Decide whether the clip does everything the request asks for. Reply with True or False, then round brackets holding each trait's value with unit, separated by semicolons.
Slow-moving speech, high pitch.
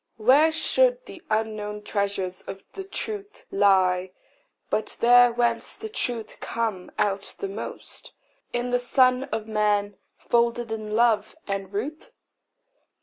True (130 wpm; 225 Hz)